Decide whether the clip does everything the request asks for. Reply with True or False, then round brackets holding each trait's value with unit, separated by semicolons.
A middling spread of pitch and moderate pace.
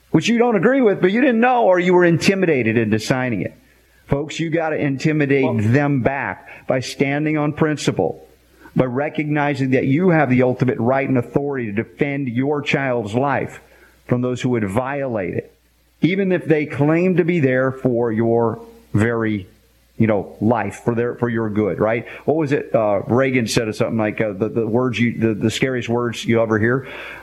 True (4.6 semitones; 190 wpm)